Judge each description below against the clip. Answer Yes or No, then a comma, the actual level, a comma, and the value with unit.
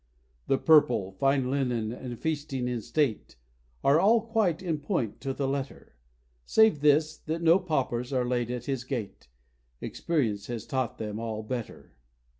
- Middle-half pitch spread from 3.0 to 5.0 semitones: Yes, average, 4.5 semitones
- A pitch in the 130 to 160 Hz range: Yes, low, 135 Hz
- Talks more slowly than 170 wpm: Yes, average, 155 wpm